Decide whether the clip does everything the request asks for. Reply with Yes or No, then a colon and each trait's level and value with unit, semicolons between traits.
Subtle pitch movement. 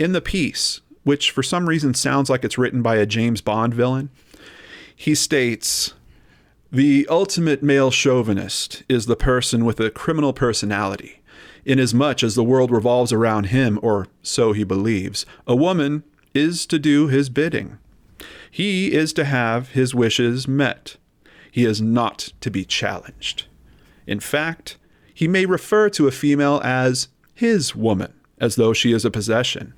No: average, 4.3 semitones